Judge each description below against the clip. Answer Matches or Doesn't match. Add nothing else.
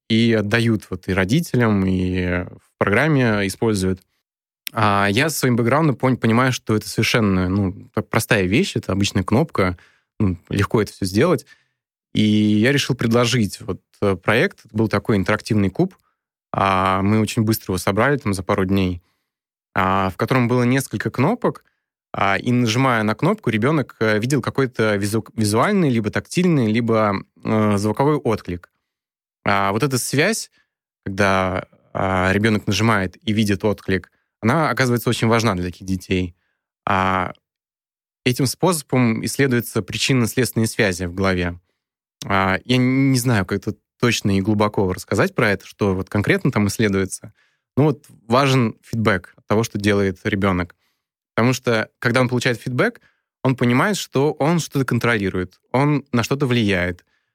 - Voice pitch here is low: Matches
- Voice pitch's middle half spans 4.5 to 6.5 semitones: Doesn't match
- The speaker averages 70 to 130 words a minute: Doesn't match